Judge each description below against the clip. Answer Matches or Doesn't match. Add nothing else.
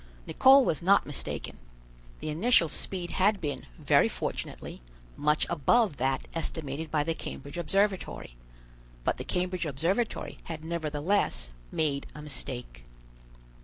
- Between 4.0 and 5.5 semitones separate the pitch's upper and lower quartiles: Matches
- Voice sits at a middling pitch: Matches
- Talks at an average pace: Doesn't match